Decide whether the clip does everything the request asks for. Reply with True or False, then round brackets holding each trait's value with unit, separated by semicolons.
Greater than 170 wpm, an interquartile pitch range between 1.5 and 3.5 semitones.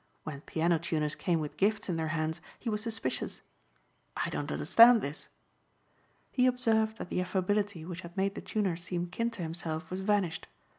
False (180 wpm; 4.6 semitones)